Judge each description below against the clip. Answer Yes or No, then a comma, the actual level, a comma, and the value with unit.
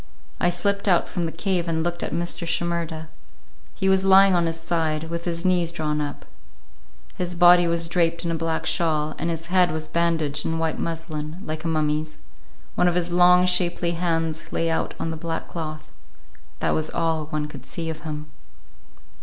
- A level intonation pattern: Yes, narrow, 1.6 semitones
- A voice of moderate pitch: Yes, medium, 165 Hz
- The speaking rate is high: No, average, 190 wpm